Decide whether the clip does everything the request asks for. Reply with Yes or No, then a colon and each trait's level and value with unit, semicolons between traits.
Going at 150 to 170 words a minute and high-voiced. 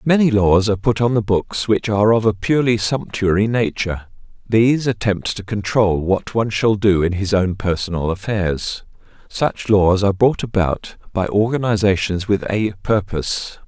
No: average, 160 wpm; low, 105 Hz